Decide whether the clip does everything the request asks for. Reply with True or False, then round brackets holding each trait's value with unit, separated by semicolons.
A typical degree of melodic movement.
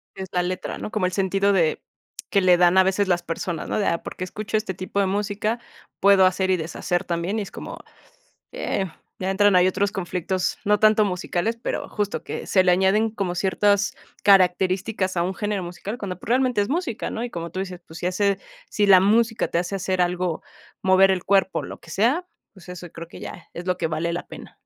False (2.2 semitones)